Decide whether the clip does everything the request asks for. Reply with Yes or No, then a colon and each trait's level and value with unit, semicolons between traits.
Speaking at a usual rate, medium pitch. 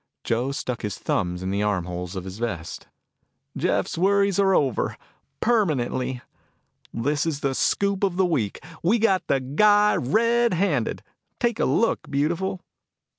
Yes: average, 150 wpm; medium, 145 Hz